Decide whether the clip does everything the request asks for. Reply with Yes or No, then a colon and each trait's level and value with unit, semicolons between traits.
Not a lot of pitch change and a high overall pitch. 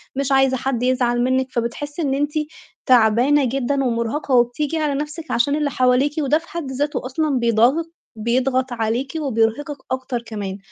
No: average, 3.2 semitones; very high, 260 Hz